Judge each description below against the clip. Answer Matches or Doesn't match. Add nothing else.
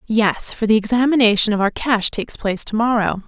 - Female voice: Matches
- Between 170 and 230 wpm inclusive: Matches